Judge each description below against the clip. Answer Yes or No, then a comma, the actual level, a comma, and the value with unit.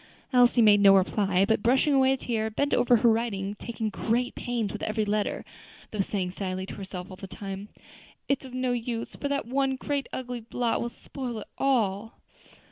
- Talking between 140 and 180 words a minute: No, average, 190 wpm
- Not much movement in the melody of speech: No, average, 3.6 semitones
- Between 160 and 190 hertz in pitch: No, high, 225 Hz